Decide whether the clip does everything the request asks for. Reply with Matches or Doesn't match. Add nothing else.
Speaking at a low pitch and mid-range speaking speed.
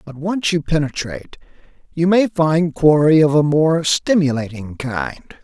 Doesn't match